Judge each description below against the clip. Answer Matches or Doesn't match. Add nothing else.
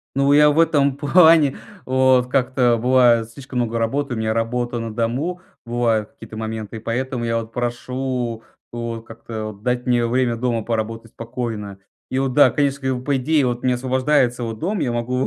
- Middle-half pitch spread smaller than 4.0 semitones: Matches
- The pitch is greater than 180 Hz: Doesn't match